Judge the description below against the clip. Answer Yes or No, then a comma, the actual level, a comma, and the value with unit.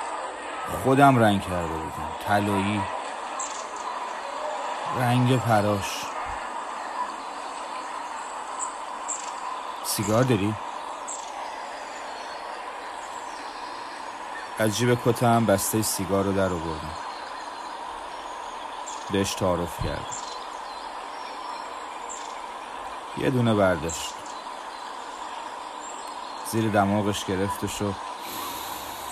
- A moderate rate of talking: No, slow, 60 wpm